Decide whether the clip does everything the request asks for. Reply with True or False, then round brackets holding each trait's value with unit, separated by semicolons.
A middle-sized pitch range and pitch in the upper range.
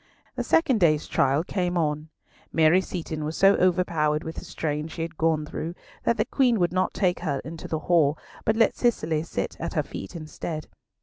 False (3.0 semitones; 165 Hz)